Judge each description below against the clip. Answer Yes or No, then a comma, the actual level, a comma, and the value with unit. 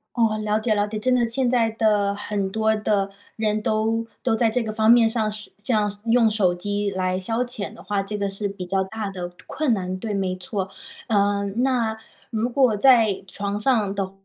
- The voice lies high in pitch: Yes, high, 215 Hz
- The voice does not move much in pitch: Yes, narrow, 2.2 semitones